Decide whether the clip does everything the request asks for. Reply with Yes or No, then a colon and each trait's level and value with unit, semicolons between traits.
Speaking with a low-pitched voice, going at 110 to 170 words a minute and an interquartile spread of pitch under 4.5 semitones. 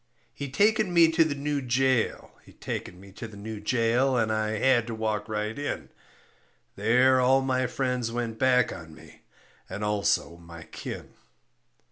Yes: low, 120 Hz; average, 165 wpm; average, 3.7 semitones